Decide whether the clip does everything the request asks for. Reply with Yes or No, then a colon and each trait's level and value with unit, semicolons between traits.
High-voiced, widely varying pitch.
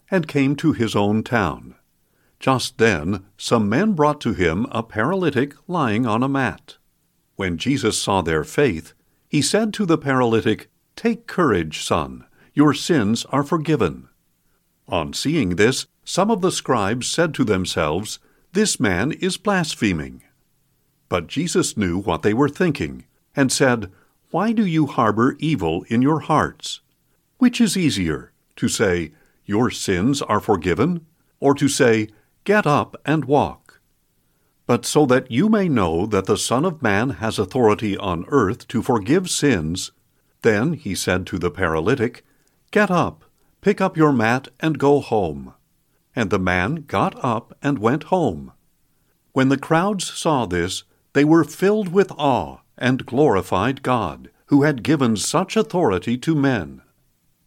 No: low, 135 Hz; wide, 7.4 semitones